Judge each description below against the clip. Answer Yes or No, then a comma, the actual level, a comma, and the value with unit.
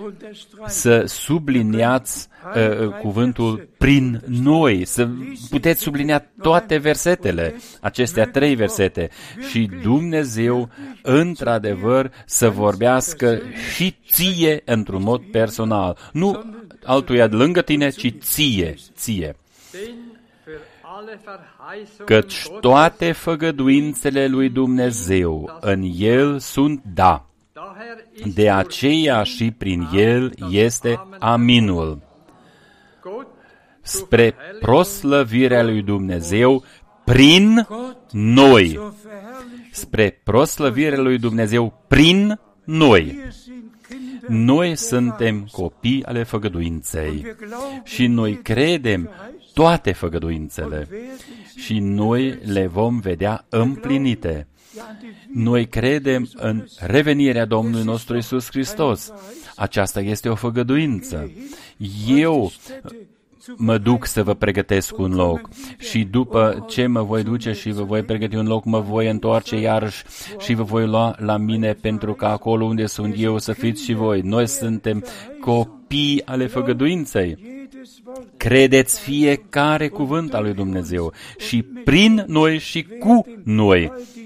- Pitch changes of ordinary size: No, wide, 6.1 semitones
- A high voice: No, low, 120 Hz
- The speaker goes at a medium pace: No, slow, 105 wpm